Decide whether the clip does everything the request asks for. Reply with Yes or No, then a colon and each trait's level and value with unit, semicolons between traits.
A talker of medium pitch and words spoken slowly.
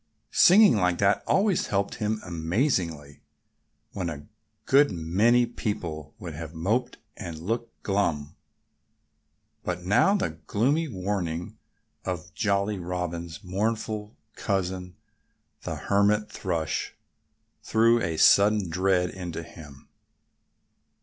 No: very low, 95 Hz; slow, 105 wpm